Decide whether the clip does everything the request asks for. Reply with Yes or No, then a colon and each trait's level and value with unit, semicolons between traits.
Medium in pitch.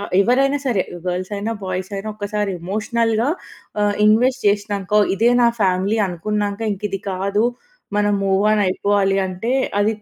No: high, 205 Hz